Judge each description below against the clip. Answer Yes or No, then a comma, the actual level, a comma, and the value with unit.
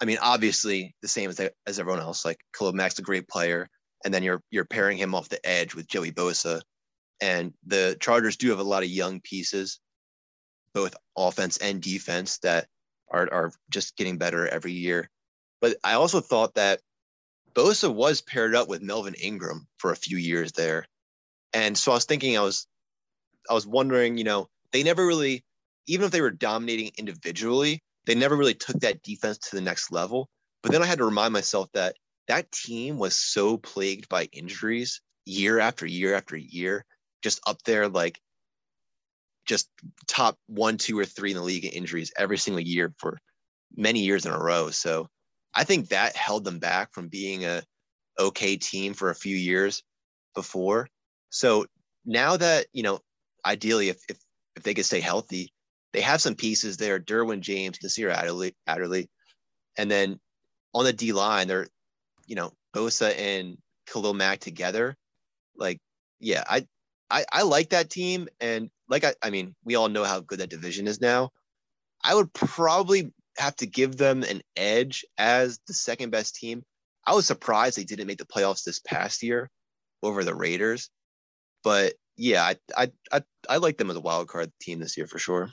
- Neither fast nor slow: Yes, average, 185 wpm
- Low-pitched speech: Yes, low, 100 Hz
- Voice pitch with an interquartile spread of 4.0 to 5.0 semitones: Yes, average, 4.4 semitones